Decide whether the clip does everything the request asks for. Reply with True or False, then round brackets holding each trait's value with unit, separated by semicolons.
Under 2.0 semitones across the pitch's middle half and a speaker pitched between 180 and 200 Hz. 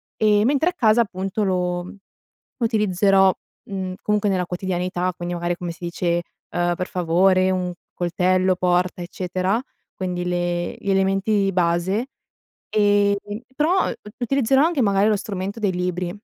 False (2.7 semitones; 185 Hz)